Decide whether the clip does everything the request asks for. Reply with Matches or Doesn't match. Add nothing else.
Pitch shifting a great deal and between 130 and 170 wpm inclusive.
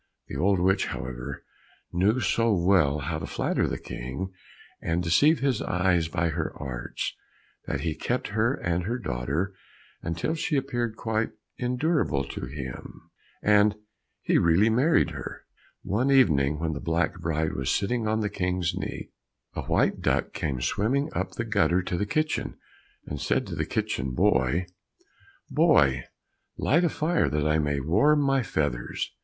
Matches